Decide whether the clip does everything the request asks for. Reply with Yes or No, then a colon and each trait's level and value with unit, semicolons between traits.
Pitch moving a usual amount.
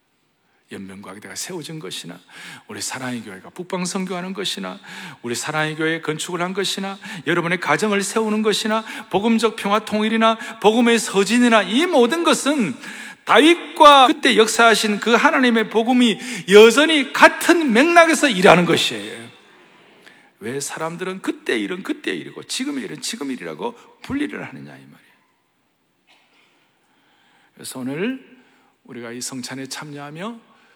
No: wide, 6.0 semitones